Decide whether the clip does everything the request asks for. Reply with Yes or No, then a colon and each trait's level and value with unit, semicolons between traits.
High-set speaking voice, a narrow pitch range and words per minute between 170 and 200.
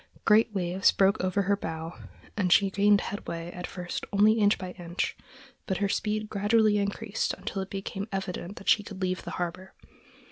Yes: high, 195 Hz; narrow, 2.2 semitones; average, 180 wpm